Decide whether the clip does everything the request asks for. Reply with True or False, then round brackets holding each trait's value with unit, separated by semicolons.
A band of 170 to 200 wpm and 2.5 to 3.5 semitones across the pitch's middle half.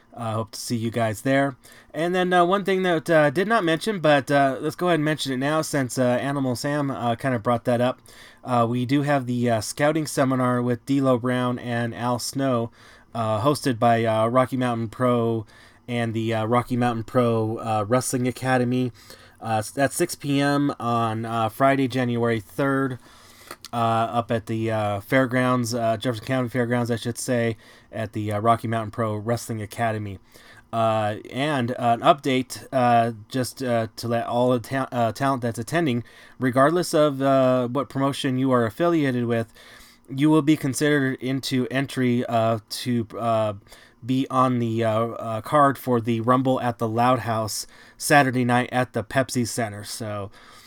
True (180 wpm; 2.8 semitones)